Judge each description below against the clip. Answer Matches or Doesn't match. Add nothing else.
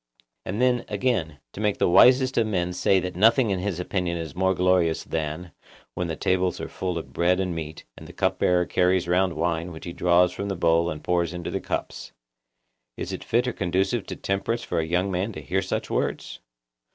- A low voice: Matches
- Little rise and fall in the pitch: Matches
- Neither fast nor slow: Doesn't match